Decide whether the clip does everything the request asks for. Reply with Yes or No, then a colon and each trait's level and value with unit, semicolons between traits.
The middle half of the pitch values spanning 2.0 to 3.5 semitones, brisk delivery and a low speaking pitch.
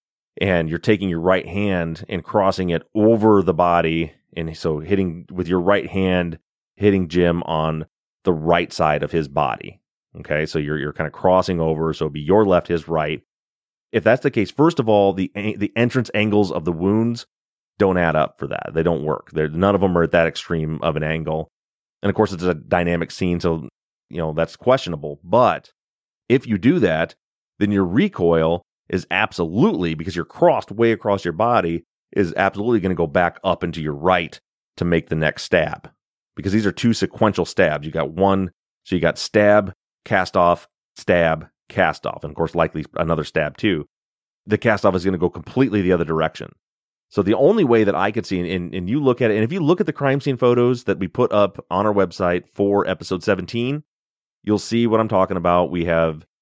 No: average, 4.0 semitones; fast, 210 wpm; very low, 90 Hz